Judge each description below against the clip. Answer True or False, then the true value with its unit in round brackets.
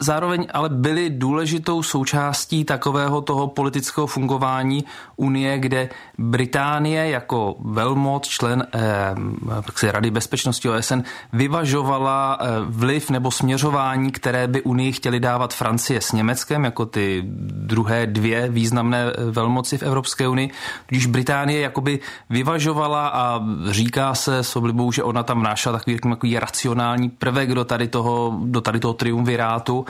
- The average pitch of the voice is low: True (130 Hz)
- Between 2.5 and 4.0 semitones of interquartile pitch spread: True (2.8 semitones)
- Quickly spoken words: False (130 wpm)